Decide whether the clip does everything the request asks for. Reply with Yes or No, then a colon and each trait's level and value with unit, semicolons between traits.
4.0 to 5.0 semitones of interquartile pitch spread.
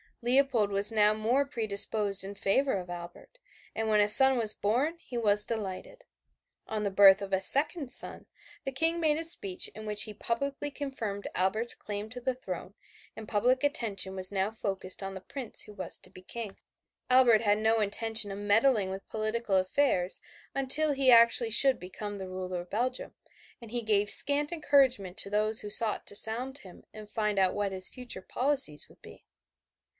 Yes: average, 4.4 semitones